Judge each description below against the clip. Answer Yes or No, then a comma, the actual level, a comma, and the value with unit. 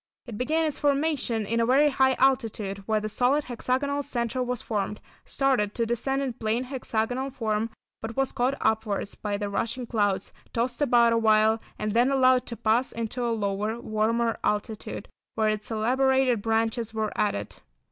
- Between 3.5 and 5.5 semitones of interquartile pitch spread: No, average, 3.1 semitones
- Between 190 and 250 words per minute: No, average, 165 wpm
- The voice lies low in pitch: No, high, 230 Hz